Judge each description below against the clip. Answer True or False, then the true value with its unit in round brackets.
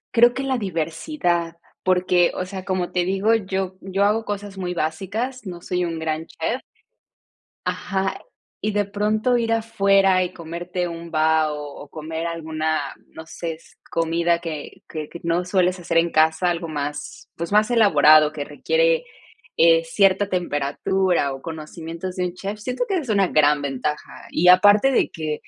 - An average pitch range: True (3.9 semitones)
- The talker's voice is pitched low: False (180 Hz)